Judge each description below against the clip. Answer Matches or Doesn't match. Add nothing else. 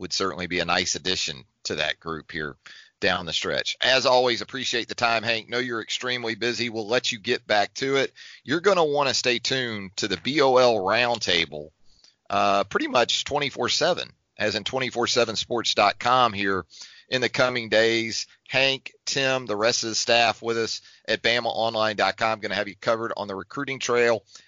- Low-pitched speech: Matches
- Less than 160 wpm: Doesn't match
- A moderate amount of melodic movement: Matches